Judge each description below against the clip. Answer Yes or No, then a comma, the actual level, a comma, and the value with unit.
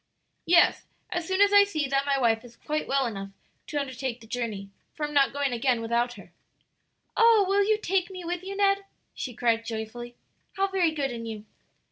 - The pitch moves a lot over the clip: Yes, wide, 7.8 semitones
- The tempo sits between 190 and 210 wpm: Yes, average, 200 wpm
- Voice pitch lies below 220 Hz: No, very high, 275 Hz